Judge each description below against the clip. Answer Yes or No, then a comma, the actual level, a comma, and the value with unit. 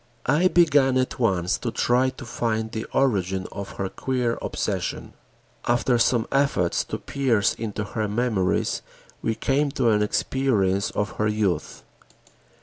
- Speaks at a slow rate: No, average, 145 wpm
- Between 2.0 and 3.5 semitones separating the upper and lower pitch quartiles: No, average, 4.2 semitones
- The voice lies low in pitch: Yes, low, 115 Hz